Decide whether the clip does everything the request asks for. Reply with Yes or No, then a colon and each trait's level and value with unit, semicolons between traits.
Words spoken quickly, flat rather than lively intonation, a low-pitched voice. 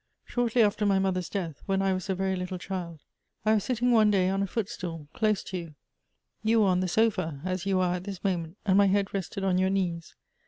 No: fast, 235 wpm; narrow, 1.9 semitones; high, 190 Hz